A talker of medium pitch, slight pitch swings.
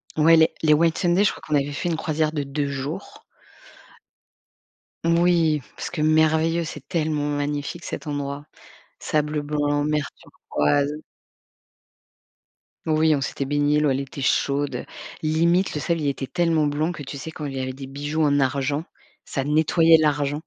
Yes: medium, 150 Hz; narrow, 1.9 semitones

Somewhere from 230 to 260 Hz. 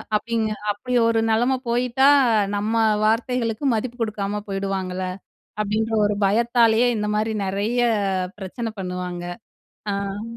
No: high, 220 Hz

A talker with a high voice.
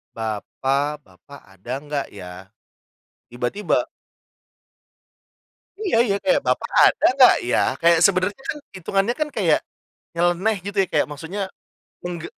No: medium, 170 Hz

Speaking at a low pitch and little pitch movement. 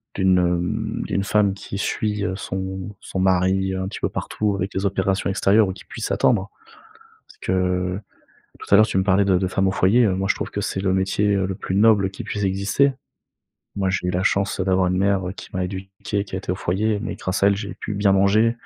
Yes: very low, 95 Hz; narrow, 1.4 semitones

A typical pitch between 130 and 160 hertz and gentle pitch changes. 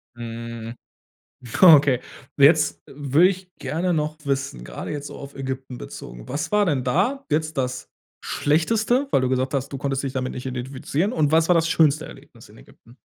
No: medium, 140 Hz; average, 3.9 semitones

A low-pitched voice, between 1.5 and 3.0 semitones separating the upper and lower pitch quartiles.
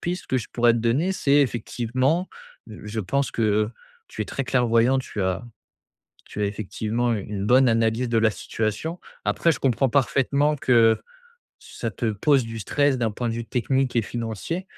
No: low, 120 Hz; average, 3.4 semitones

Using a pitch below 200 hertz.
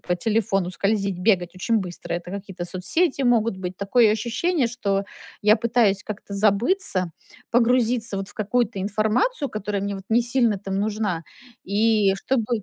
No: high, 210 Hz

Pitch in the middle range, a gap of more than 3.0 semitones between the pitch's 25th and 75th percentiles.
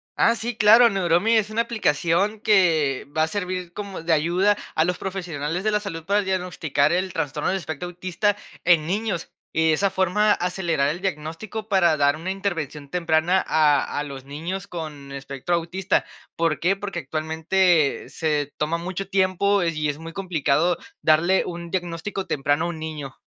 Yes: medium, 175 Hz; average, 3.6 semitones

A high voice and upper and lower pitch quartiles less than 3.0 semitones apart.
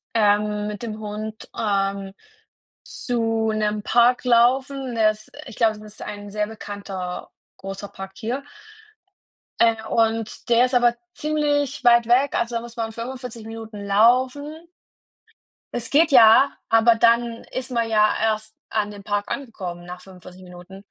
Yes: high, 225 Hz; narrow, 2.5 semitones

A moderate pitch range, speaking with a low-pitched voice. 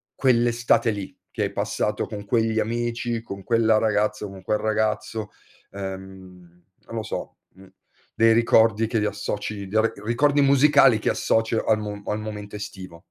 No: narrow, 2.0 semitones; low, 110 Hz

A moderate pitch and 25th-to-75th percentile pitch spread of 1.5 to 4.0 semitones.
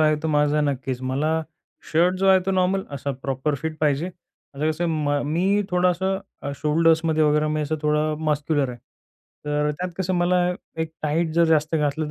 Yes: medium, 155 Hz; narrow, 2.5 semitones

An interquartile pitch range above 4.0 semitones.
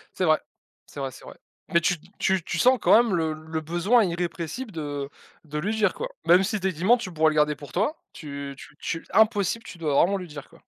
Yes: average, 4.9 semitones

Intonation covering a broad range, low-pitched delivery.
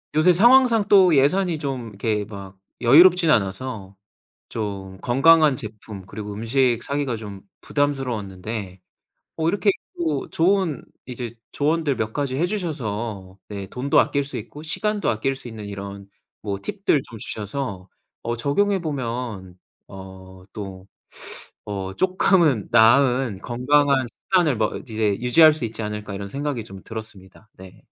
Yes: wide, 6.5 semitones; low, 120 Hz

